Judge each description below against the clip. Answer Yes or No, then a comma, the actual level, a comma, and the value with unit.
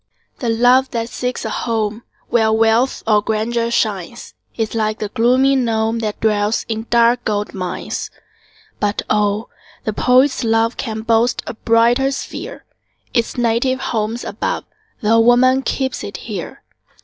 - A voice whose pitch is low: No, high, 230 Hz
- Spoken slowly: No, average, 145 wpm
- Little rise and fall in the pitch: Yes, narrow, 1.9 semitones